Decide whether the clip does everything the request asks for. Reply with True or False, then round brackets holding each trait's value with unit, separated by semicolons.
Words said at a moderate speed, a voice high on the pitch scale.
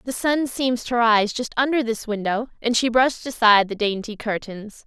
True (195 wpm; 230 Hz)